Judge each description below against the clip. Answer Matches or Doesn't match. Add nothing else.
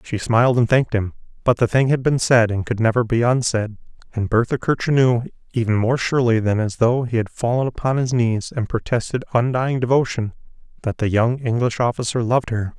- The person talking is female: Doesn't match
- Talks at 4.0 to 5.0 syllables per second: Doesn't match